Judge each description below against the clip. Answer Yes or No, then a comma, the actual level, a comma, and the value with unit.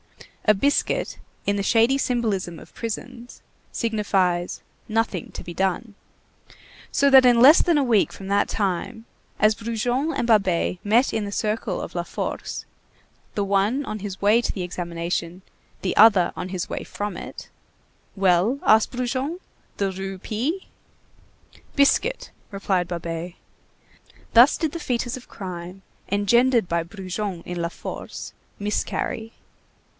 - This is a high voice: Yes, high, 210 Hz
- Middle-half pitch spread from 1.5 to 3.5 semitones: No, average, 4.5 semitones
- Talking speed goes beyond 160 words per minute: No, average, 140 wpm